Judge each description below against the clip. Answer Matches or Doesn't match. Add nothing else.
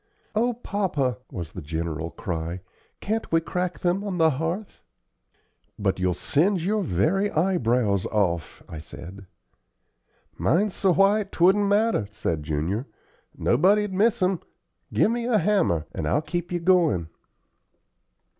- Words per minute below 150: Matches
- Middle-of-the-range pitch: Matches